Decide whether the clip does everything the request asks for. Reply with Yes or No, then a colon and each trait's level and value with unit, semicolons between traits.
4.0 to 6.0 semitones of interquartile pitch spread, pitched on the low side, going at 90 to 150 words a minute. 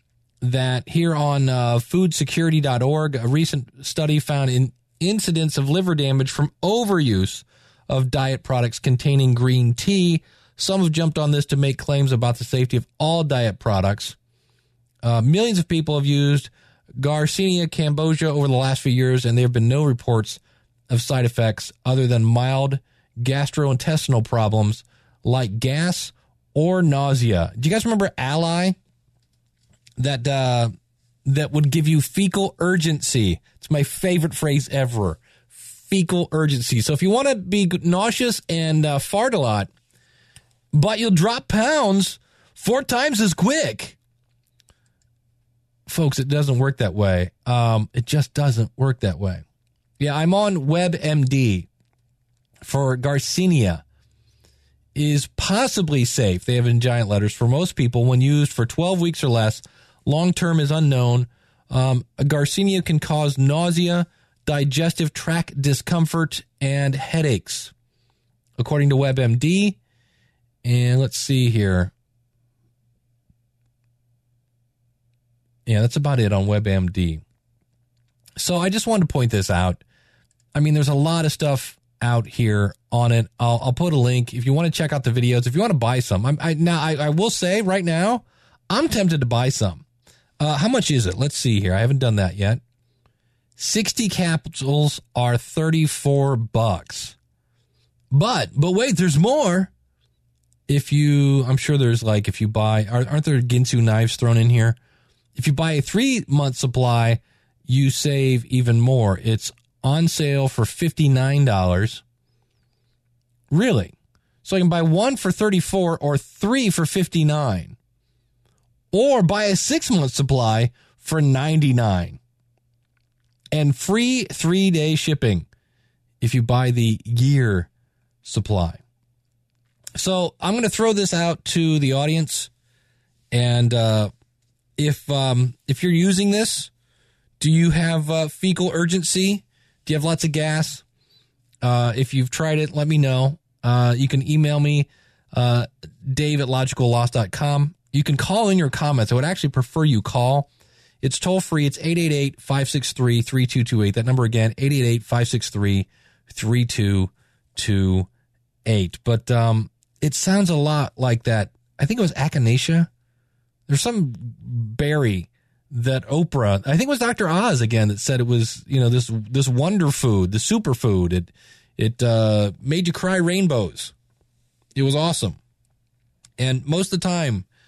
Yes: average, 4.4 semitones; low, 130 Hz; average, 145 wpm